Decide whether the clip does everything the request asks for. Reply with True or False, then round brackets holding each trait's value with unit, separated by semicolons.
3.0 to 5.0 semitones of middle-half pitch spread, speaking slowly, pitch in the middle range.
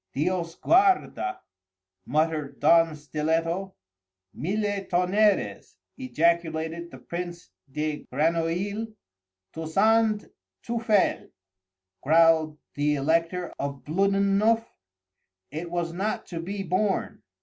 True (3.8 semitones; 85 wpm; 170 Hz)